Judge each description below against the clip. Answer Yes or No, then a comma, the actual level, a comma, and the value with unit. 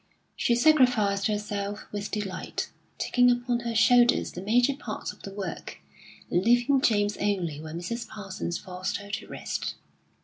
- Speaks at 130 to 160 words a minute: Yes, average, 145 wpm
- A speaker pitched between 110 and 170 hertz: No, high, 210 Hz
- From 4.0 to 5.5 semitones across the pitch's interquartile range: No, average, 3.5 semitones